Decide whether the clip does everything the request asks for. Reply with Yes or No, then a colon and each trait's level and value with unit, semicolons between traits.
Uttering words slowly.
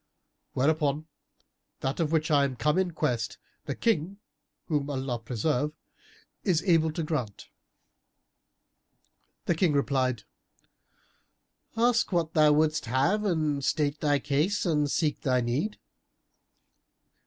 Yes: slow, 120 wpm